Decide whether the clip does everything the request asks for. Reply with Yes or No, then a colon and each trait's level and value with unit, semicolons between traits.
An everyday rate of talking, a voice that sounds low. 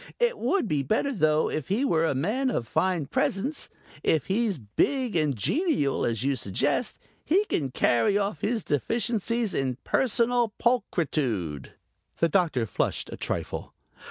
No: average, 150 wpm; medium, 185 Hz